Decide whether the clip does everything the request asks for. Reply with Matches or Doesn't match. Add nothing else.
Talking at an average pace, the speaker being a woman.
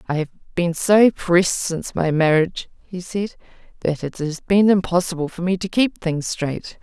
Matches